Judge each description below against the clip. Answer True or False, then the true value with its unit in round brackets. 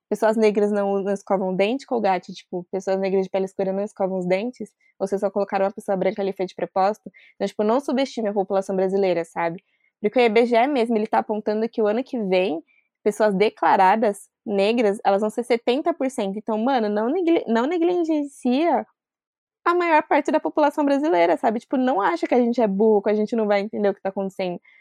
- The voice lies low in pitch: False (215 Hz)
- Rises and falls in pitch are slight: False (4.2 semitones)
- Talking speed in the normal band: False (210 wpm)